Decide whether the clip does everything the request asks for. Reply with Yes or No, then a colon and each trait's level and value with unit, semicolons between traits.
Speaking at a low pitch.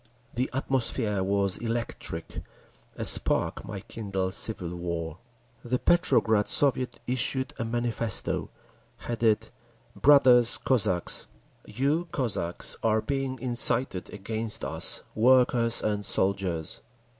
Yes: low, 115 Hz